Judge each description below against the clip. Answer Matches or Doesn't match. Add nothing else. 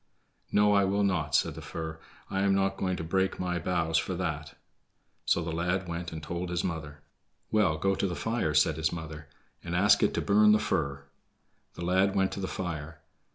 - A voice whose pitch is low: Matches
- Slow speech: Doesn't match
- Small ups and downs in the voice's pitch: Doesn't match